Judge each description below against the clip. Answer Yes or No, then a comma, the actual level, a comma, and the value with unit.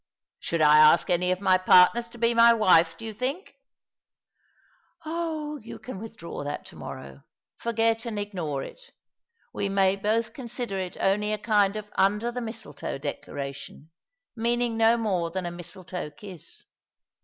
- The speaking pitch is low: No, high, 205 Hz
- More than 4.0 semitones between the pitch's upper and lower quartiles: Yes, average, 4.7 semitones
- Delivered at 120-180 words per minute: Yes, average, 165 wpm